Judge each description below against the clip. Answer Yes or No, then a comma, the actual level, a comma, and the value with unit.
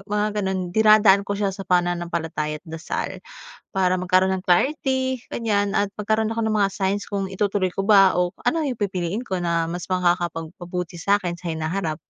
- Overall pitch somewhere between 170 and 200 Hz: Yes, high, 190 Hz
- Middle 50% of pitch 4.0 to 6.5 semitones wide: No, average, 2.8 semitones